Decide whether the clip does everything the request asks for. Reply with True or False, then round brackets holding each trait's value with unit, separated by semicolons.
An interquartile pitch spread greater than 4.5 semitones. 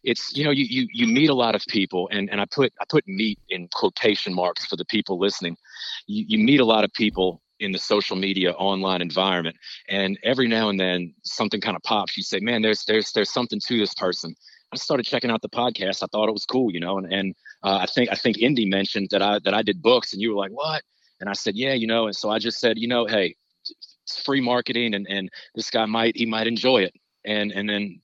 False (3.2 semitones)